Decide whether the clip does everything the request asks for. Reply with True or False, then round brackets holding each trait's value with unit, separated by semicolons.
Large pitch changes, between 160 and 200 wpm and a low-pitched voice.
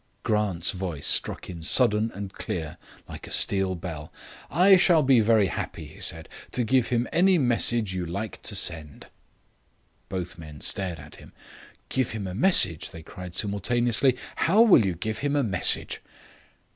True (5.8 semitones; 165 wpm; 100 Hz)